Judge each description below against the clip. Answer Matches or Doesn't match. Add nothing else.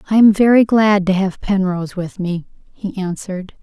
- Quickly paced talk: Doesn't match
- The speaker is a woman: Matches